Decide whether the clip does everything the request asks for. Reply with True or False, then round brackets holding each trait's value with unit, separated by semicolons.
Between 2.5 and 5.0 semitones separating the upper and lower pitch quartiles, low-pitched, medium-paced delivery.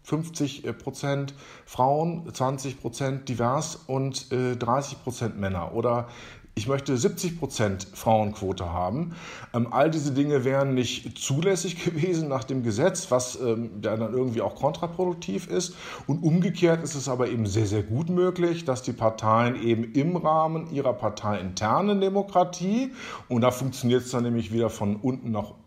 False (5.5 semitones; 130 Hz; 145 wpm)